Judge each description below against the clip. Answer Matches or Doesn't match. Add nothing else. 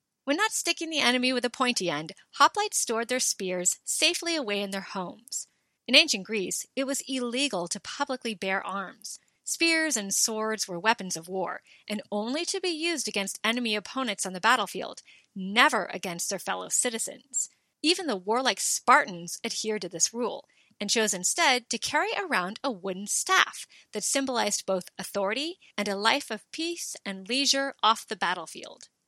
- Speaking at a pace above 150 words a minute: Matches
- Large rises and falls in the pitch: Matches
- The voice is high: Matches